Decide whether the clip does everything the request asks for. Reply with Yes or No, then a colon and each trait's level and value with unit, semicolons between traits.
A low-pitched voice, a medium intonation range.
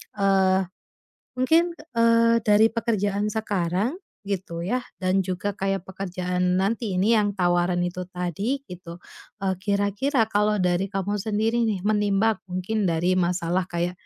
No: high, 195 Hz; average, 3.0 semitones